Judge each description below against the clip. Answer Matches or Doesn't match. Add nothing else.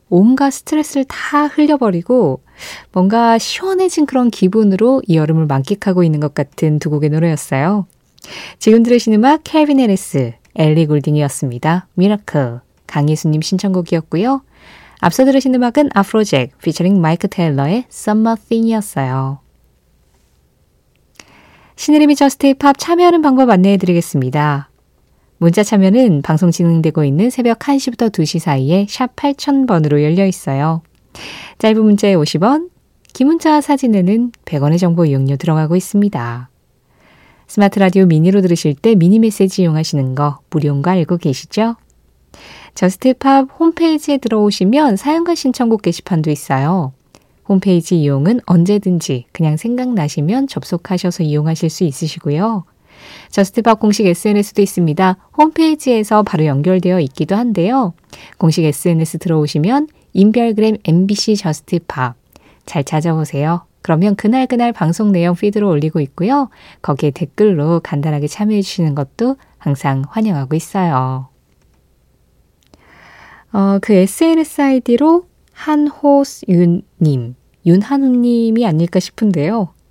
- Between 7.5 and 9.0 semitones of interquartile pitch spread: Doesn't match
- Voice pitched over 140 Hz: Matches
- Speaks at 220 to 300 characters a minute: Doesn't match